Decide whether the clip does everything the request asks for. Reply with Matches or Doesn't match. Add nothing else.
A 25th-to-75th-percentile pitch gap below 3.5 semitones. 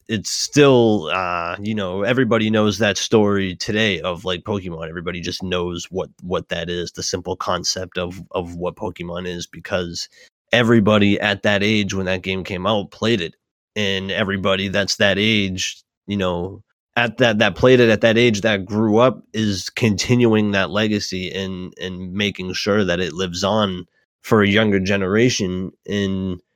Matches